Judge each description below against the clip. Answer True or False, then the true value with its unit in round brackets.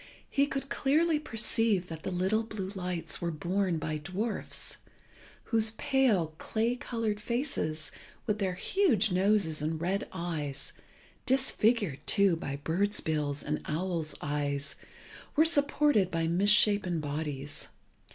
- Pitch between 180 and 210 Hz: True (190 Hz)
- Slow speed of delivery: True (125 wpm)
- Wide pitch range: True (5.9 semitones)